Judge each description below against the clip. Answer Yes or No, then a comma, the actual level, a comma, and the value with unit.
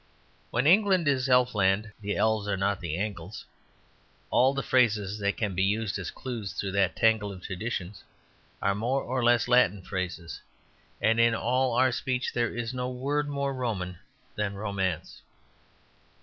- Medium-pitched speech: No, low, 110 Hz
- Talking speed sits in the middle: Yes, average, 160 wpm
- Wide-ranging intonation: No, average, 4.3 semitones